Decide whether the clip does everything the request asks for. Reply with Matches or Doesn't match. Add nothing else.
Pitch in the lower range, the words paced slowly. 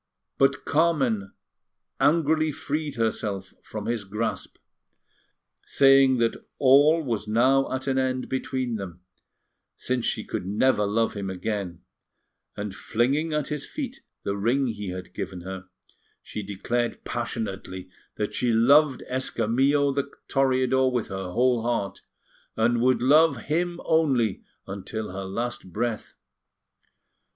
Matches